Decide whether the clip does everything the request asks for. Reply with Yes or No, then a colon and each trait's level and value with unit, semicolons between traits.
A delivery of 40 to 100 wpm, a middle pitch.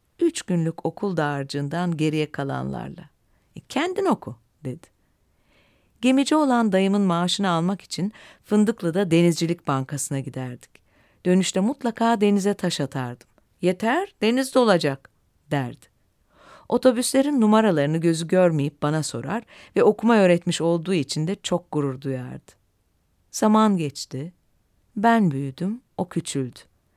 No: average, 110 wpm; medium, 175 Hz